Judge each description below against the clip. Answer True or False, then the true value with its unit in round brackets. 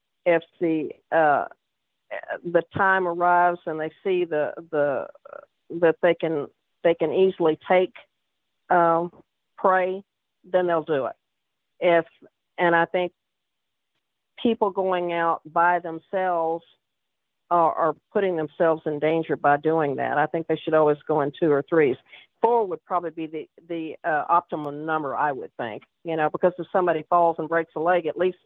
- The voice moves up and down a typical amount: False (2.1 semitones)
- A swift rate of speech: False (160 wpm)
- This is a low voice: False (170 Hz)